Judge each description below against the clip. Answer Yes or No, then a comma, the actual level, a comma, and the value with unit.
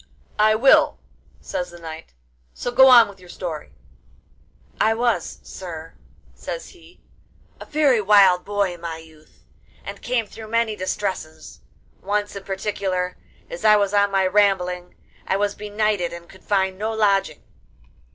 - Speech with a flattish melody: No, average, 3.2 semitones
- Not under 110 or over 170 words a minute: Yes, average, 150 wpm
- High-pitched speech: Yes, high, 200 Hz